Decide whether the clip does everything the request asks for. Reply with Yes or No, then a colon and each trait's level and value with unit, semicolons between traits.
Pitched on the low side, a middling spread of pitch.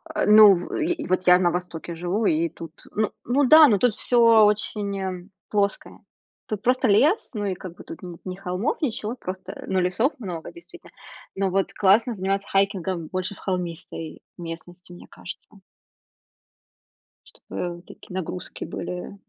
No: high, 190 Hz; average, 3.2 semitones